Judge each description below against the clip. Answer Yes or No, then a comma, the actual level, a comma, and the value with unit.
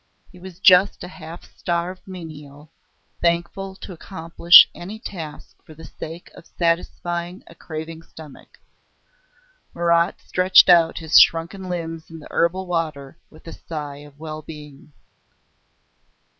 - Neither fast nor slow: No, slow, 130 wpm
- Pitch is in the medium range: Yes, medium, 170 Hz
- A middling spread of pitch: No, narrow, 2.2 semitones